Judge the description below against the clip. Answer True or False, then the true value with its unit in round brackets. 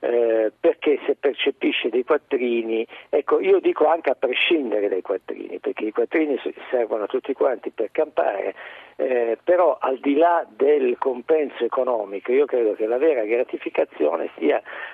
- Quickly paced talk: False (155 wpm)